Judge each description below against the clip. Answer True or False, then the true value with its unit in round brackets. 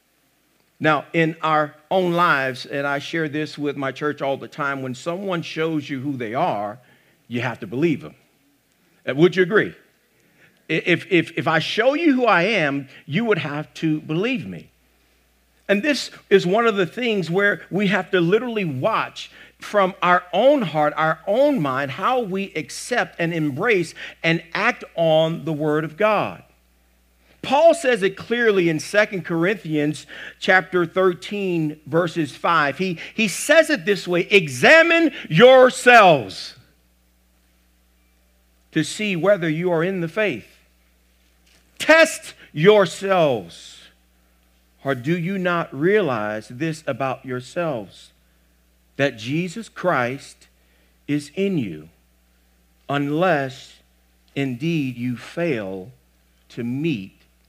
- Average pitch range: False (8.2 semitones)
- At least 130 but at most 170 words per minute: True (135 wpm)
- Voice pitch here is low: False (155 Hz)